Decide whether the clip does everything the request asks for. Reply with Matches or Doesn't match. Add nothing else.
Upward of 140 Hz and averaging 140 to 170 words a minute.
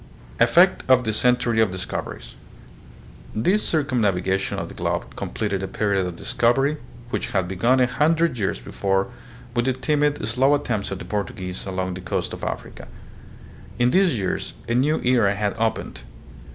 Doesn't match